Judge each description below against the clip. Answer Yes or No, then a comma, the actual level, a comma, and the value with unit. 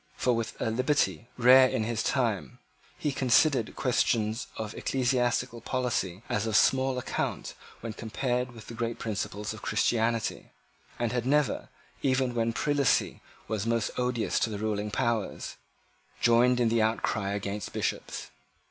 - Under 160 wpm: Yes, average, 145 wpm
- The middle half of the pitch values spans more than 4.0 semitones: No, narrow, 2.5 semitones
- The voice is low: Yes, low, 115 Hz